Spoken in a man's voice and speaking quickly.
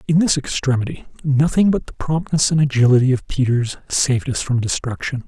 No: male; average, 170 wpm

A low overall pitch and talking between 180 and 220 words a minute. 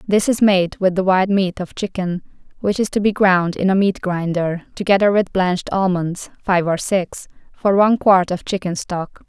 No: high, 190 Hz; average, 200 wpm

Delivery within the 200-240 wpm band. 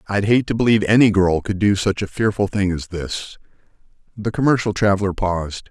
No: average, 190 wpm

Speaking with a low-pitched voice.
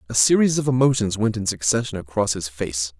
Yes: low, 105 Hz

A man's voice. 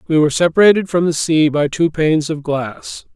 Yes: male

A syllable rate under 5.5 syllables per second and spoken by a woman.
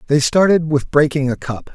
No: 5.2 syllables/s; male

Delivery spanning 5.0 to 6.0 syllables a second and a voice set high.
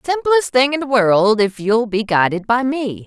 No: 4.4 syllables/s; high, 235 Hz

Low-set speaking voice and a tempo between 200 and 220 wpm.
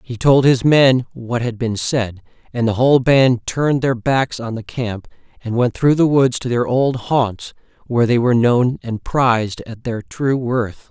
Yes: low, 125 Hz; fast, 205 wpm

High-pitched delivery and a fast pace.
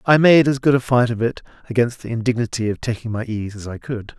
No: low, 120 Hz; fast, 260 wpm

